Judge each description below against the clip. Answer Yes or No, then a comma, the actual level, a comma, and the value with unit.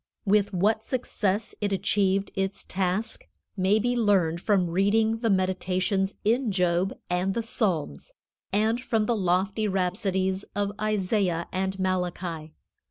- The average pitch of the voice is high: Yes, high, 195 Hz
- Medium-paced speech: No, slow, 130 wpm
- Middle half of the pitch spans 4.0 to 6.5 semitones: No, narrow, 2.4 semitones